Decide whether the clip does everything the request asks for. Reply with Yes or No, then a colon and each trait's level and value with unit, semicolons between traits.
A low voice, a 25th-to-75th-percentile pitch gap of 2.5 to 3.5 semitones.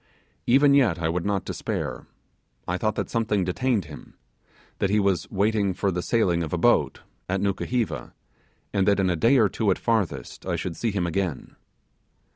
No: low, 100 Hz; average, 3.9 semitones